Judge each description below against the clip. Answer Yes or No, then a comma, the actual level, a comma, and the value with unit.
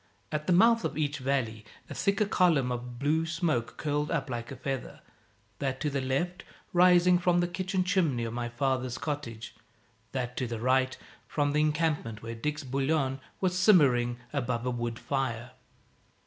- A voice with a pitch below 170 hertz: Yes, medium, 140 Hz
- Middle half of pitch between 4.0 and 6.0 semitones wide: Yes, average, 5.2 semitones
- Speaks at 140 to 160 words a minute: No, average, 170 wpm